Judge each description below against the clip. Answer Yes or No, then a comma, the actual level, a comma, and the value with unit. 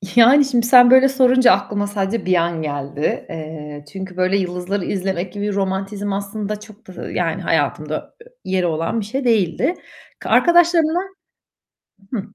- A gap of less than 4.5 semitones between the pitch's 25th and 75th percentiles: No, average, 5.0 semitones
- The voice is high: Yes, high, 200 Hz